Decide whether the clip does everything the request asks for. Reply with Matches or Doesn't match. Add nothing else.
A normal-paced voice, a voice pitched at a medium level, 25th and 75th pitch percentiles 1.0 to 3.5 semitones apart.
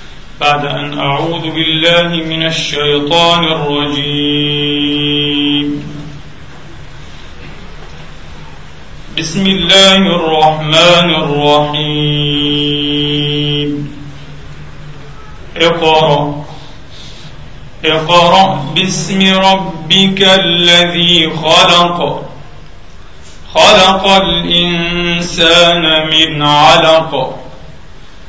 Doesn't match